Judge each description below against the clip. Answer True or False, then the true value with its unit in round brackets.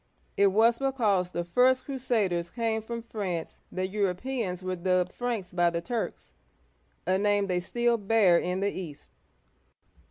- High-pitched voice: True (200 Hz)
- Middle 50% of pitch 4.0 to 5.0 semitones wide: True (4.4 semitones)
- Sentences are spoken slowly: False (150 wpm)